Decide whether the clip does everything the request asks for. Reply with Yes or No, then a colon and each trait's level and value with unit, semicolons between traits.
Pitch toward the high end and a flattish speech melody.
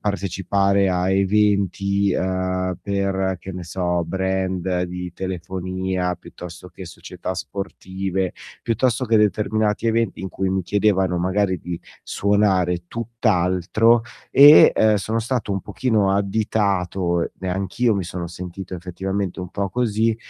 No: very low, 95 Hz; narrow, 2.1 semitones